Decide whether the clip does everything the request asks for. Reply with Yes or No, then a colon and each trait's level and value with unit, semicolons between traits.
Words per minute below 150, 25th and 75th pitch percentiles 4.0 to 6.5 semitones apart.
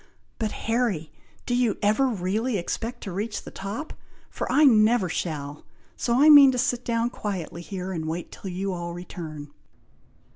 No: average, 170 wpm; wide, 5.5 semitones